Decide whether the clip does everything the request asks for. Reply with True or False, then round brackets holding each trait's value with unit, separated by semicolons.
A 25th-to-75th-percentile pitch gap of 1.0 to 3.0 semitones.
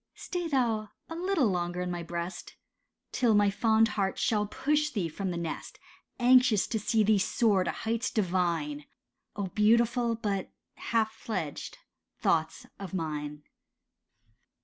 False (4.6 semitones)